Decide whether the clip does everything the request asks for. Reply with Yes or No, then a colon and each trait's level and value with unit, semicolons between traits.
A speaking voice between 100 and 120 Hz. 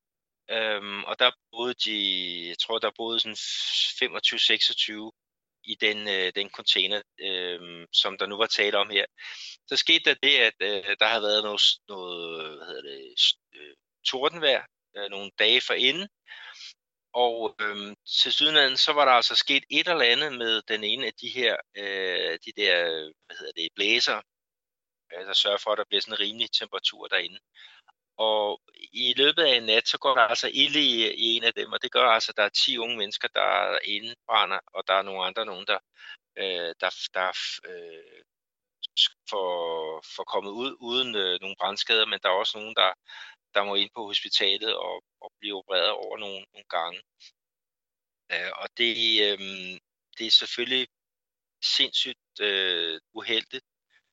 Yes: low, 115 Hz